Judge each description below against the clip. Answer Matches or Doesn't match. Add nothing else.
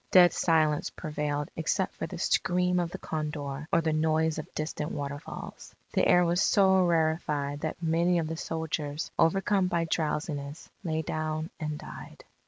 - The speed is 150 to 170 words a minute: Matches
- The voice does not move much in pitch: Matches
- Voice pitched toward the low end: Doesn't match